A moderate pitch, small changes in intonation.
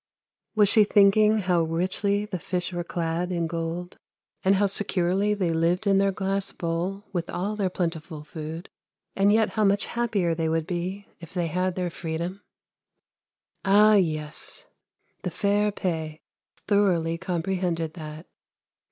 No: medium, 180 Hz; average, 3.2 semitones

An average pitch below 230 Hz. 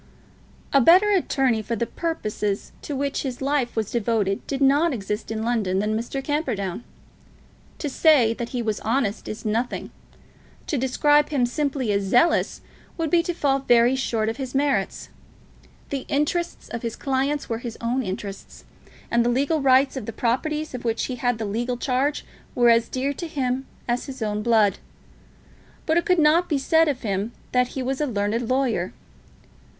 No: very high, 250 Hz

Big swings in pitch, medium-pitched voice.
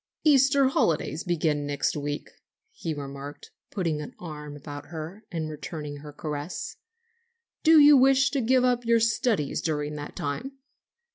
Yes: wide, 9.0 semitones; medium, 160 Hz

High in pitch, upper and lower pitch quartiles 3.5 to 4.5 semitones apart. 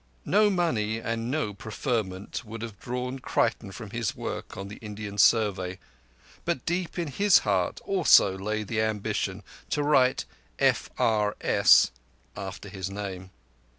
No: low, 110 Hz; average, 4.1 semitones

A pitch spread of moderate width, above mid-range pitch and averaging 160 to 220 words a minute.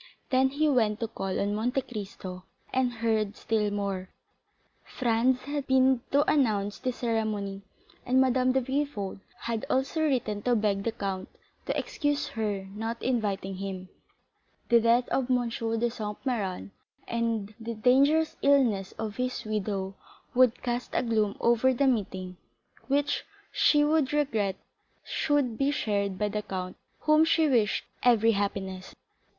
No: average, 4.2 semitones; high, 230 Hz; average, 145 wpm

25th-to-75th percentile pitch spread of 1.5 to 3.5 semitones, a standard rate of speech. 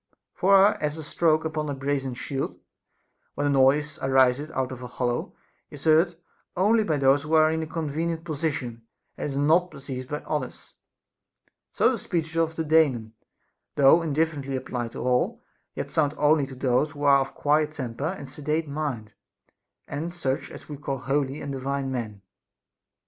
Yes: average, 2.9 semitones; average, 175 wpm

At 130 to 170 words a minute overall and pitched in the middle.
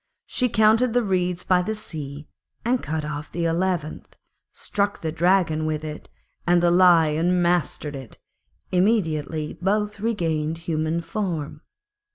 Yes: slow, 135 wpm; medium, 175 Hz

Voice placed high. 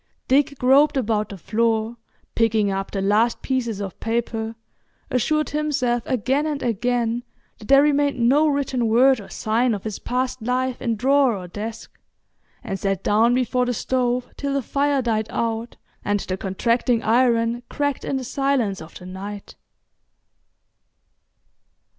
Yes: high, 235 Hz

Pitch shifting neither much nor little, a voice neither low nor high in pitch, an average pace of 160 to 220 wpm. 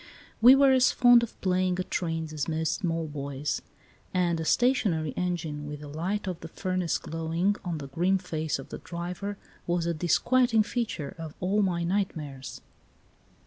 Yes: average, 3.6 semitones; medium, 175 Hz; average, 170 wpm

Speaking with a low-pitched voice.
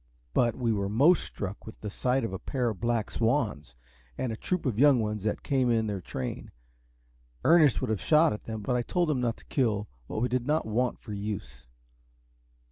Yes: low, 115 Hz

